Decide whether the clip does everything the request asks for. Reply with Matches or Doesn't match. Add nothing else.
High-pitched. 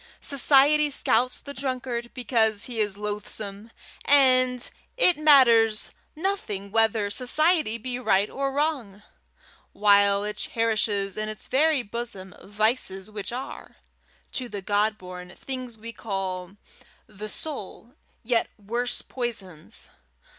Matches